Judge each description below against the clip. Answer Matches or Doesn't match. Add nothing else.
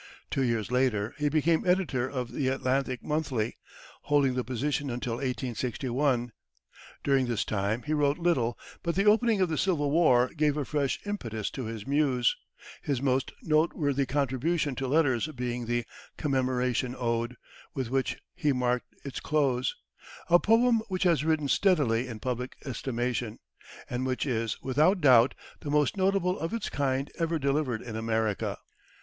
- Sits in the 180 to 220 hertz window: Doesn't match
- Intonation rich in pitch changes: Doesn't match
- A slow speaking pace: Doesn't match